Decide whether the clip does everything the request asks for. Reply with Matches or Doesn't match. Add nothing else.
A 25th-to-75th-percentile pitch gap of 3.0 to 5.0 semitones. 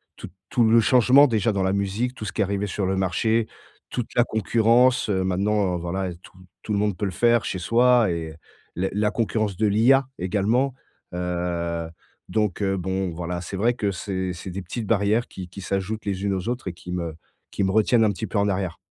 Matches